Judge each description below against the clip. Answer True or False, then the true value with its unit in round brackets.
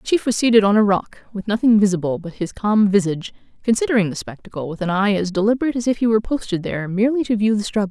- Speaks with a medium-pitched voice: False (210 Hz)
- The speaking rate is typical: False (250 wpm)